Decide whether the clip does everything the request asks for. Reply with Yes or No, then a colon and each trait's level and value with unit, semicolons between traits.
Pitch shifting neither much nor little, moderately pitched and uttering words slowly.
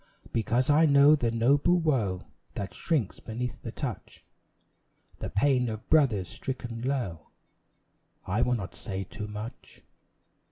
No: average, 4.9 semitones; low, 120 Hz; slow, 130 wpm